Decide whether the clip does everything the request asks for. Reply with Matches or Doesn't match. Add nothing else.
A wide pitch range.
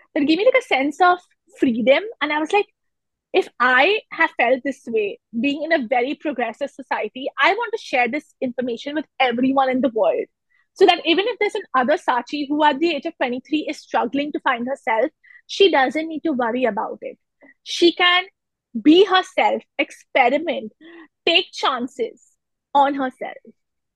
Matches